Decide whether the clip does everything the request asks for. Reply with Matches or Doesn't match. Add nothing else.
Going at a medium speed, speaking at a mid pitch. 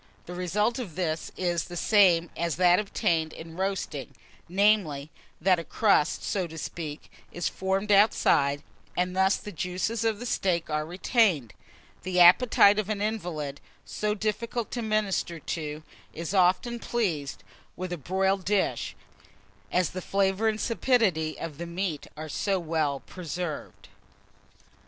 Matches